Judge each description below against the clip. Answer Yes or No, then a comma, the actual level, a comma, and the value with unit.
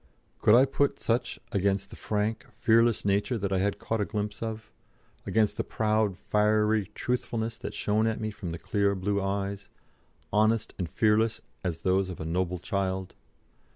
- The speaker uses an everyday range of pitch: No, narrow, 2.2 semitones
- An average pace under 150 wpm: No, average, 170 wpm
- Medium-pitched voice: No, low, 105 Hz